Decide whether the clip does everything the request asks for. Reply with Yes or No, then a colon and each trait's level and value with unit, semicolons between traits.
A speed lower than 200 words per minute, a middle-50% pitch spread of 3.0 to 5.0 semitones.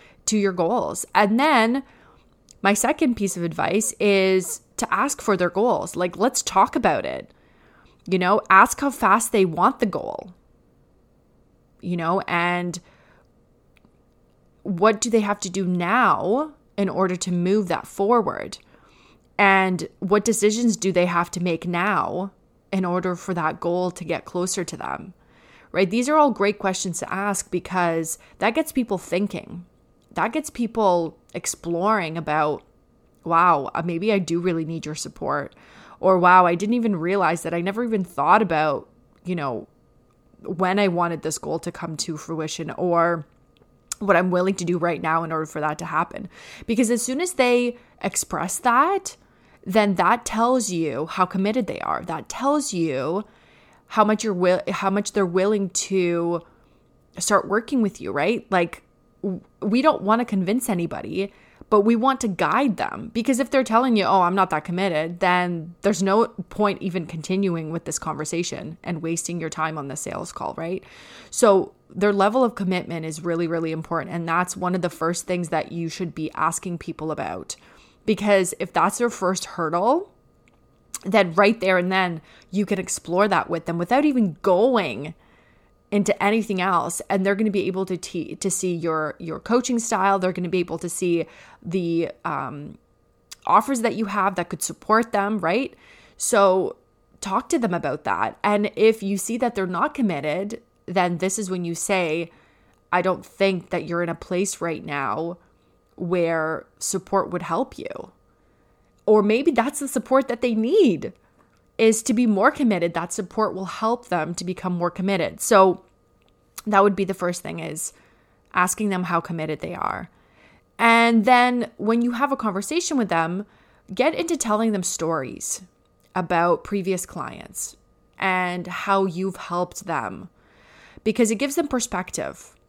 Yes: average, 170 wpm; average, 3.9 semitones